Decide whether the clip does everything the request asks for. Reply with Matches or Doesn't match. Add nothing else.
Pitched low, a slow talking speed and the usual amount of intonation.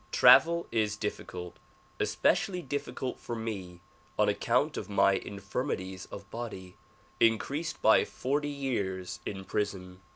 Doesn't match